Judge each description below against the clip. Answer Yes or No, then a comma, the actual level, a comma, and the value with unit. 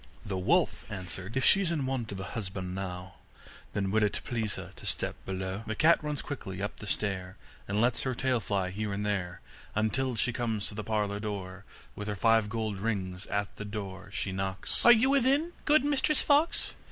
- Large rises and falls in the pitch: No, average, 4.3 semitones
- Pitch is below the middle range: Yes, low, 105 Hz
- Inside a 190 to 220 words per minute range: Yes, average, 200 wpm